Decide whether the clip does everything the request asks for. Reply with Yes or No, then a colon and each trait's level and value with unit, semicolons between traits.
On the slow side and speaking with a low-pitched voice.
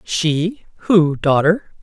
No: slow, 100 wpm; medium, 170 Hz